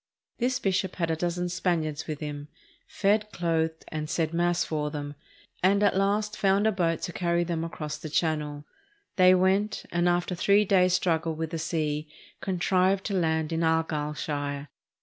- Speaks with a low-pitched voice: No, medium, 170 Hz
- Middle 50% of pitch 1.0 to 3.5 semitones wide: Yes, average, 3.1 semitones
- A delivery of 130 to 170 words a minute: No, average, 180 wpm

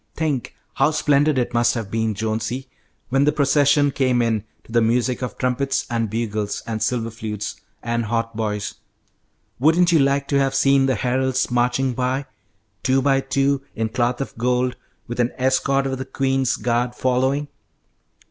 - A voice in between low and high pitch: No, low, 125 Hz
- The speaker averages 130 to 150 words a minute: No, average, 165 wpm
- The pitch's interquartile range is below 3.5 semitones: Yes, average, 2.7 semitones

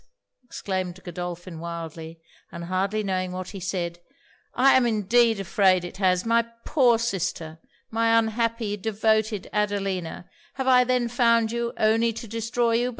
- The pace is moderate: Yes, average, 145 wpm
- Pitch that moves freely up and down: No, average, 4.1 semitones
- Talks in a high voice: Yes, high, 210 Hz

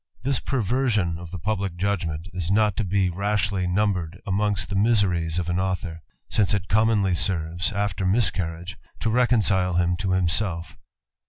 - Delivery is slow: Yes, slow, 120 wpm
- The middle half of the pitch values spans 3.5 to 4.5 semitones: No, average, 3.1 semitones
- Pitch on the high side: No, very low, 95 Hz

